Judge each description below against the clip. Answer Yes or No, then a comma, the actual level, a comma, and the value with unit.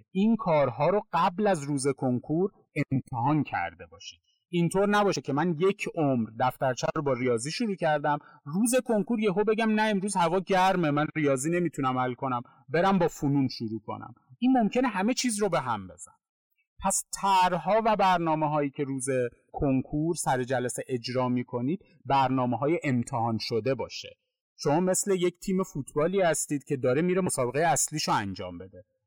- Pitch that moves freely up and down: Yes, wide, 6.7 semitones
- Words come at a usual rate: No, fast, 165 wpm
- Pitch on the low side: No, medium, 155 Hz